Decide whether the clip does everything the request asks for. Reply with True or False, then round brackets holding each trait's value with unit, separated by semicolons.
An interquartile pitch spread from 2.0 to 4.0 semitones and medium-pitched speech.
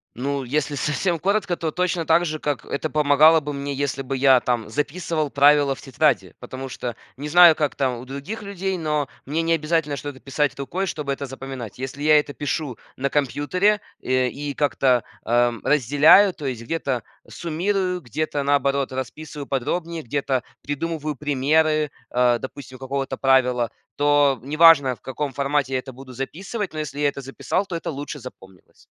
True (2.8 semitones; 145 Hz)